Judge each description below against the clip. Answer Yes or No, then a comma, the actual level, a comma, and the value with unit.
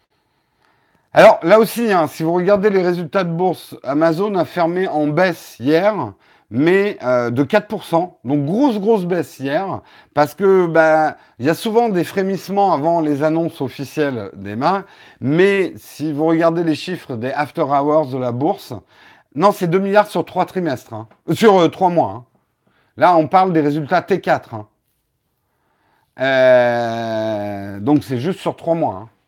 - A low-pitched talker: No, medium, 160 Hz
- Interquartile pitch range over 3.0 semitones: Yes, average, 5.1 semitones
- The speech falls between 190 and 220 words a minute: No, average, 165 wpm